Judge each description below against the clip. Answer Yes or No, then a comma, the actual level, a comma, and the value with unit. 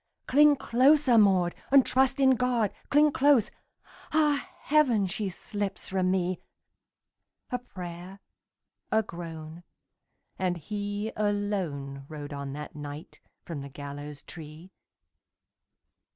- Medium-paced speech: No, slow, 110 wpm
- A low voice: No, high, 195 Hz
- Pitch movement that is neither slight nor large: No, wide, 7.7 semitones